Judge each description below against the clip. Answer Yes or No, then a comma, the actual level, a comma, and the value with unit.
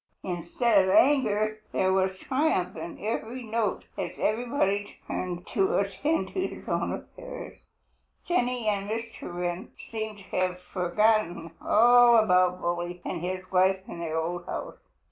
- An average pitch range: Yes, average, 4.1 semitones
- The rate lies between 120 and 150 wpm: Yes, average, 145 wpm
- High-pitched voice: Yes, high, 195 Hz